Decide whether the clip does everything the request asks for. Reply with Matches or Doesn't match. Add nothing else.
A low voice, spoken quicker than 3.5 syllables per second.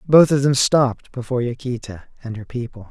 Matches